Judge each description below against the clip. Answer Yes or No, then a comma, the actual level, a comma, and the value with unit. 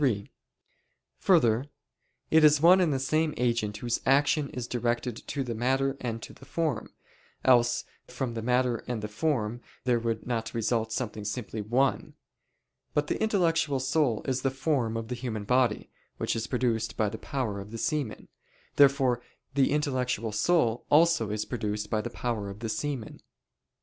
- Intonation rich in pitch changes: No, average, 3.7 semitones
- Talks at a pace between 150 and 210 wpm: Yes, average, 170 wpm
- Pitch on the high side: No, low, 125 Hz